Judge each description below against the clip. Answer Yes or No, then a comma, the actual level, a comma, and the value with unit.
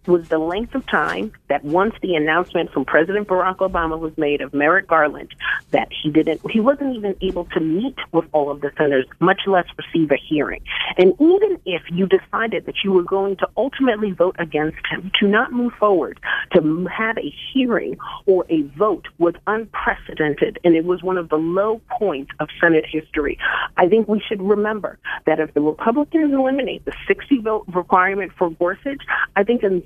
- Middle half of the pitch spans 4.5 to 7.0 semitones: Yes, average, 5.2 semitones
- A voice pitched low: No, medium, 185 Hz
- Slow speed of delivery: No, average, 190 wpm